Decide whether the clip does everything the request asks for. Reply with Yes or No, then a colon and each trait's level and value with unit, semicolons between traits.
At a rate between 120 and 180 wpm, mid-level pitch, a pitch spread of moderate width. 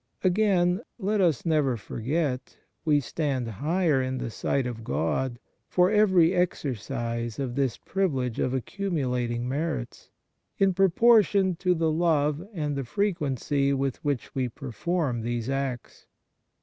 No: slow, 135 wpm; medium, 145 Hz; wide, 6.1 semitones